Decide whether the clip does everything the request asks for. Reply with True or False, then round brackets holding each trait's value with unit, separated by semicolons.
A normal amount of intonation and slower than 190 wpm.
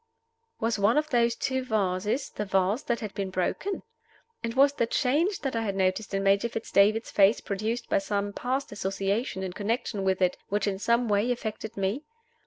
False (3.3 semitones; 195 wpm)